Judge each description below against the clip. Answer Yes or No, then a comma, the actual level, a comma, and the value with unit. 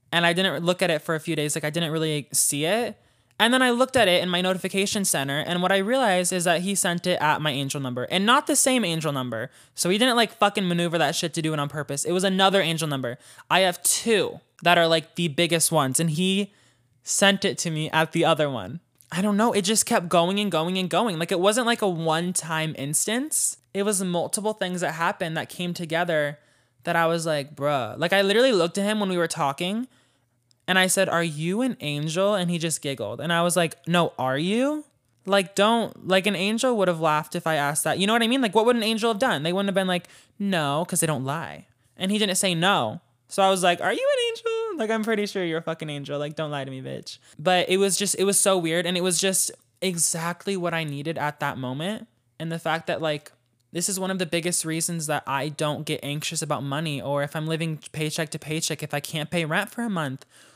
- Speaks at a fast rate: Yes, fast, 255 wpm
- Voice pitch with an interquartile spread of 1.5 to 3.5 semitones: No, average, 4.2 semitones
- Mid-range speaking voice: Yes, medium, 170 Hz